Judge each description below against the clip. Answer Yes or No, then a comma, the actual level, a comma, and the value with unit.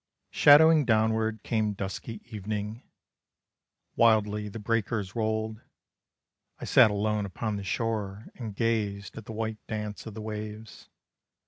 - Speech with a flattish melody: Yes, narrow, 1.3 semitones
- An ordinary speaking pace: No, slow, 125 wpm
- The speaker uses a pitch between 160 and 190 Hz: No, low, 110 Hz